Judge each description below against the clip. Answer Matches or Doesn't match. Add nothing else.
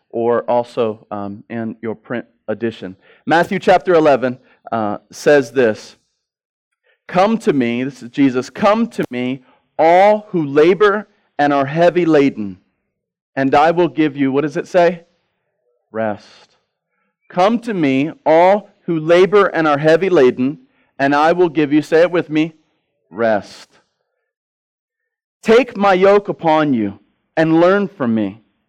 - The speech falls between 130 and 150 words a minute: Matches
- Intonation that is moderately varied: Doesn't match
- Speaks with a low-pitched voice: Doesn't match